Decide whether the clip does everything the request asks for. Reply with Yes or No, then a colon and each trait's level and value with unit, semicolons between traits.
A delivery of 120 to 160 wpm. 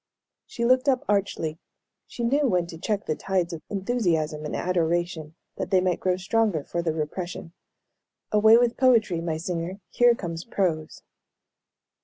Yes: average, 155 wpm